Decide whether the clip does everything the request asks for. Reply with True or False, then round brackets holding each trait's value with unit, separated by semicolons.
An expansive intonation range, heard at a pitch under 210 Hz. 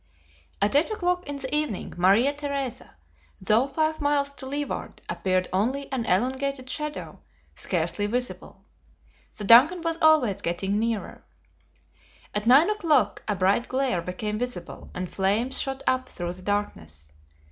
False (5.9 semitones; 250 Hz)